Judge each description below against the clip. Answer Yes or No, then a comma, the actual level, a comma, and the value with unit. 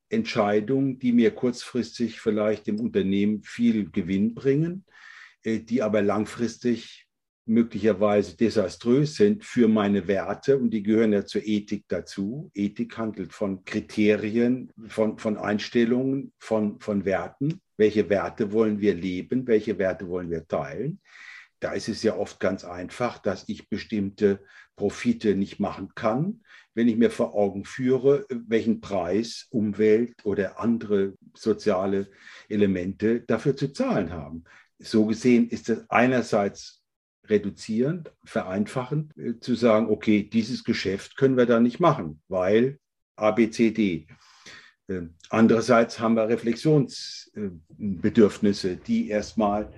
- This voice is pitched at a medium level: No, low, 110 Hz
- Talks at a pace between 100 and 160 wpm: Yes, slow, 125 wpm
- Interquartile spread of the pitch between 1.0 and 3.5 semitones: Yes, average, 2.8 semitones